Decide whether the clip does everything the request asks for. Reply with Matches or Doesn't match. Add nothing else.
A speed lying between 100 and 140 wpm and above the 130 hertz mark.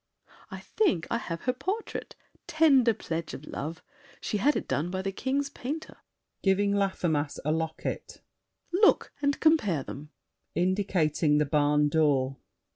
Matches